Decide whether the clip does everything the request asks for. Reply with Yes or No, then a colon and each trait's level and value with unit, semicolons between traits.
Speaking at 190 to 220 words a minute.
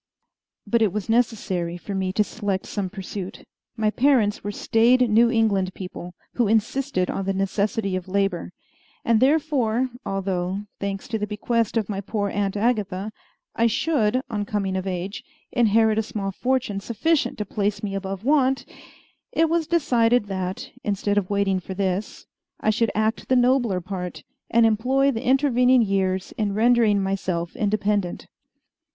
No: average, 160 wpm